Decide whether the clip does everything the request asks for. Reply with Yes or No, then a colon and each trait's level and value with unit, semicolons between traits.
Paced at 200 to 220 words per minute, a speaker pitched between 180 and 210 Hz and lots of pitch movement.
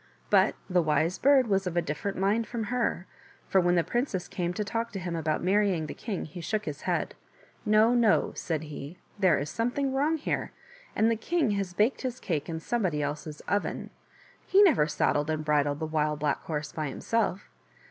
Yes: fast, 205 wpm; medium, 185 Hz; wide, 6.5 semitones